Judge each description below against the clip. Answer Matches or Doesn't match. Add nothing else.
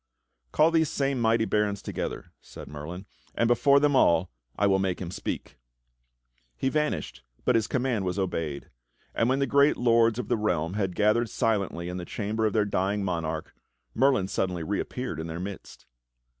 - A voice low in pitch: Matches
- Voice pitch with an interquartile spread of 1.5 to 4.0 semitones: Doesn't match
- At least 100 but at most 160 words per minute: Doesn't match